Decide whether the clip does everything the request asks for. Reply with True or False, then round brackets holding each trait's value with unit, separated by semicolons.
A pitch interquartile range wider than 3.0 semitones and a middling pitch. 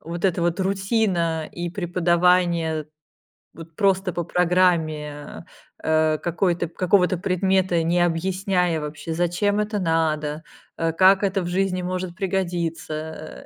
False (2.4 semitones; 175 Hz)